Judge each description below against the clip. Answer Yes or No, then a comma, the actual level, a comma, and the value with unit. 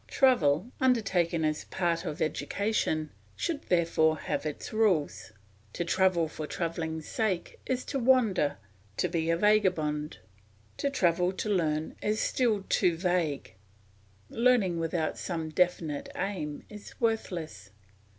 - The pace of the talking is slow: Yes, slow, 130 wpm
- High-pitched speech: No, medium, 175 Hz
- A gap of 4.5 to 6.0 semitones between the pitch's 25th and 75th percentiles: Yes, average, 5.0 semitones